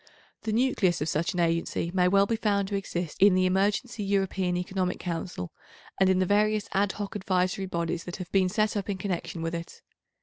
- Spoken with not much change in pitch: Yes, narrow, 2.3 semitones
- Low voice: No, high, 190 Hz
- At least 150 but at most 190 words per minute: No, fast, 205 wpm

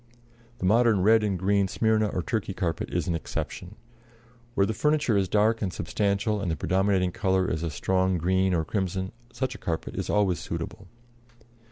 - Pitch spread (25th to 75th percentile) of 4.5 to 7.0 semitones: No, average, 2.7 semitones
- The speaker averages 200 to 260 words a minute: No, average, 180 wpm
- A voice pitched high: No, very low, 95 Hz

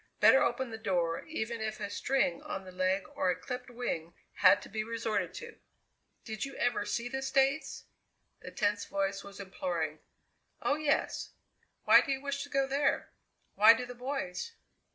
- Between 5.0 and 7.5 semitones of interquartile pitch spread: Yes, wide, 5.4 semitones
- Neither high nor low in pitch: No, high, 225 Hz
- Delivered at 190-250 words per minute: No, average, 175 wpm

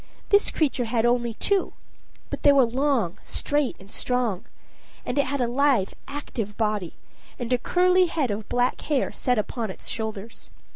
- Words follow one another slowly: No, average, 165 wpm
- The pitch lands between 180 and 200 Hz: No, high, 245 Hz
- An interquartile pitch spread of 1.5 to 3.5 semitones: No, average, 4.4 semitones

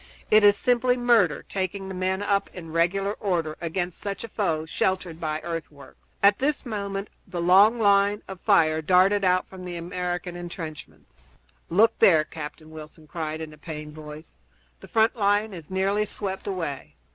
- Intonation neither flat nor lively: Yes, average, 4.0 semitones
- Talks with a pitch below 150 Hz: No, medium, 185 Hz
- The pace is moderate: Yes, average, 170 wpm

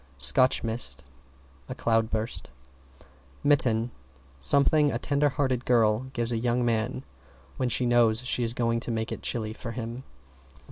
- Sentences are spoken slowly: No, average, 145 wpm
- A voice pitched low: Yes, low, 120 Hz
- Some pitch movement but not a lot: No, narrow, 2.1 semitones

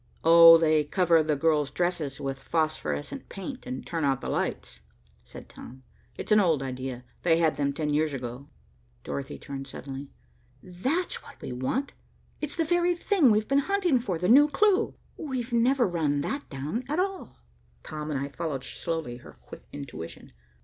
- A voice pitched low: No, medium, 165 Hz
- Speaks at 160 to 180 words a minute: Yes, average, 170 wpm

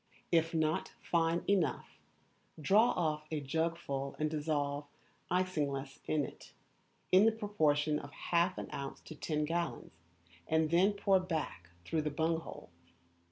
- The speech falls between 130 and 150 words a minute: Yes, average, 140 wpm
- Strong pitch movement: No, average, 2.8 semitones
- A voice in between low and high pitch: Yes, medium, 160 Hz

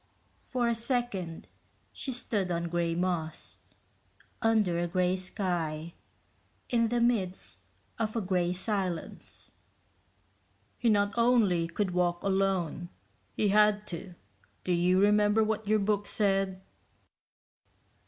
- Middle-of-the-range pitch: No, high, 195 Hz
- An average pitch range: Yes, average, 3.5 semitones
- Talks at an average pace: No, slow, 115 wpm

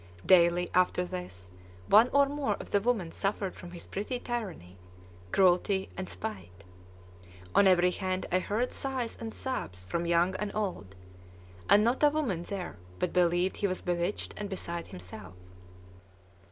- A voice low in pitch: No, medium, 185 Hz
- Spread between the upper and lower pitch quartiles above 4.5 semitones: No, average, 3.7 semitones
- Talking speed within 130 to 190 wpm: Yes, average, 155 wpm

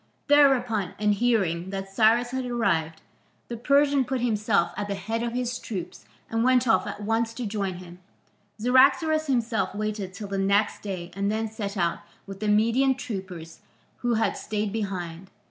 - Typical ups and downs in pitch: Yes, average, 3.8 semitones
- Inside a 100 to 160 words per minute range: No, average, 170 wpm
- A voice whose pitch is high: Yes, high, 215 Hz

